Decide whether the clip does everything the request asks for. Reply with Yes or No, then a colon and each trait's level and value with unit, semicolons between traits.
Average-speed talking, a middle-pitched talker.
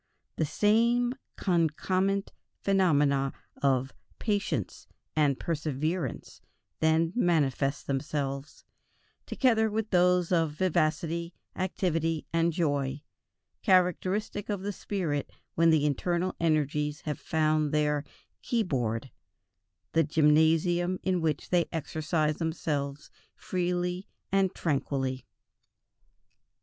No: slow, 90 wpm; medium, 160 Hz